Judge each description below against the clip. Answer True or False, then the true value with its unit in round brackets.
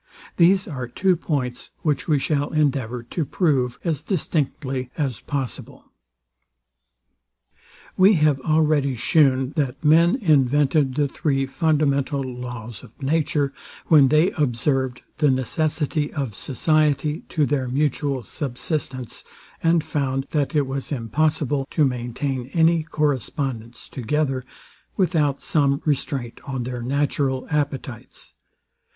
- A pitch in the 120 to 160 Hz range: True (140 Hz)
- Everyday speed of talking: False (115 wpm)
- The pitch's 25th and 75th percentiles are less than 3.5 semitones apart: True (2.9 semitones)